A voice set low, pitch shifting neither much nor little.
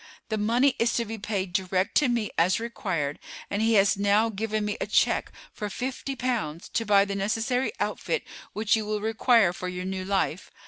No: high, 210 Hz; average, 3.1 semitones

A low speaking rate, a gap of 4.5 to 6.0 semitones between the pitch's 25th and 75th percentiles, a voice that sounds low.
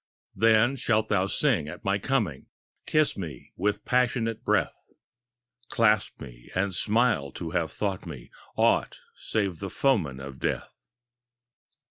Yes: slow, 130 wpm; wide, 5.6 semitones; low, 100 Hz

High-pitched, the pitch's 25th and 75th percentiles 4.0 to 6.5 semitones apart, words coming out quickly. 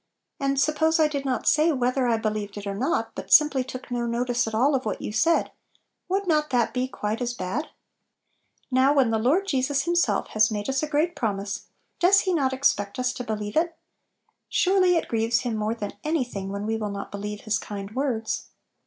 Yes: very high, 250 Hz; wide, 5.6 semitones; fast, 215 wpm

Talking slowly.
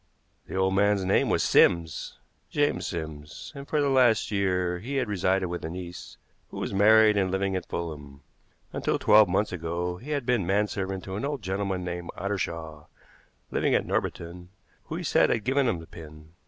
No: average, 185 wpm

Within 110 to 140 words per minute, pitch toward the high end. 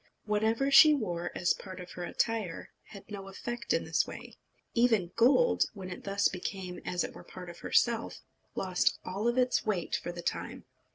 No: average, 185 wpm; high, 200 Hz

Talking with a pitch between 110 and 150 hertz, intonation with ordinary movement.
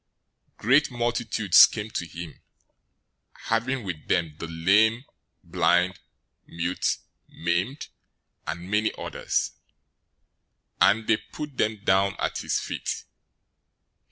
No: low, 100 Hz; average, 4.7 semitones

